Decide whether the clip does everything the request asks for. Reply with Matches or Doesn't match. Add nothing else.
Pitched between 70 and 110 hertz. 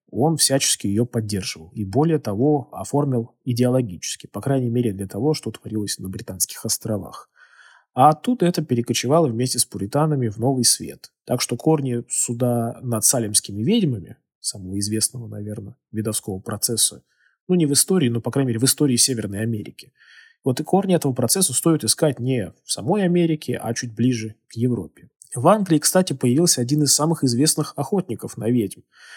Doesn't match